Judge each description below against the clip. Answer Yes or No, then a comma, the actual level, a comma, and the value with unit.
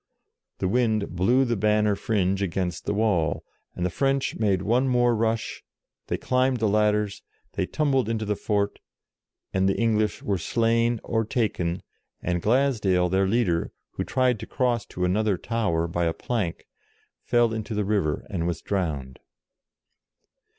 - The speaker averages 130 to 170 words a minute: Yes, average, 155 wpm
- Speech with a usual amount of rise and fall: Yes, average, 4.0 semitones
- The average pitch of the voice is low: Yes, low, 105 Hz